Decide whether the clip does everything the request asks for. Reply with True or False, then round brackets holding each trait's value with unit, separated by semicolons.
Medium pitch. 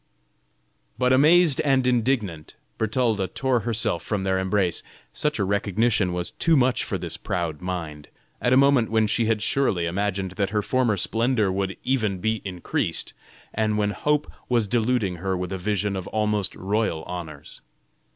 False (105 Hz)